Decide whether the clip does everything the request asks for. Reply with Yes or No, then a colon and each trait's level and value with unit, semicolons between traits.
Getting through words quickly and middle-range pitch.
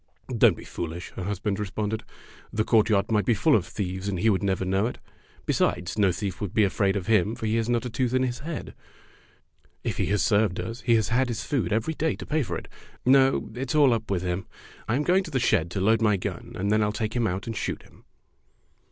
No: fast, 255 wpm; low, 110 Hz